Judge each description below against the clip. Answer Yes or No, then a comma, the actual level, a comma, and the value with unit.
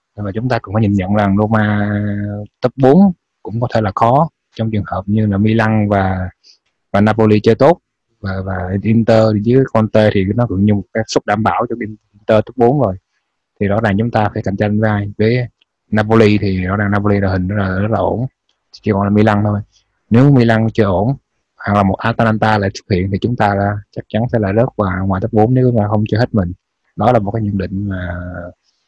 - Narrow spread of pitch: Yes, narrow, 2.1 semitones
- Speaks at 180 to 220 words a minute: No, average, 235 wpm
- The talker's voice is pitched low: Yes, low, 105 Hz